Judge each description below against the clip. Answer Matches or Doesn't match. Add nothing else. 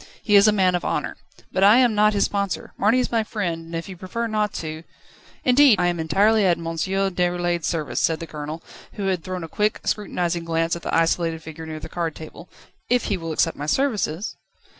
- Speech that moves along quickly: Matches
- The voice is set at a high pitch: Doesn't match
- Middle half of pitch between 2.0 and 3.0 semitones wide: Doesn't match